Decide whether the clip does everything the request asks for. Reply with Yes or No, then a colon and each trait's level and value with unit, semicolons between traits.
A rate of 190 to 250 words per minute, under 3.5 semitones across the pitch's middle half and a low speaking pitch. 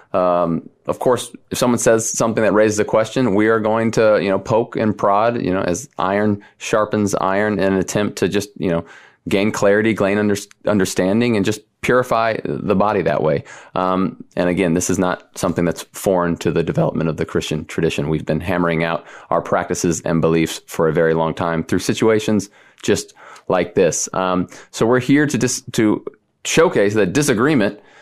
No: average, 195 wpm; average, 3.8 semitones; low, 100 Hz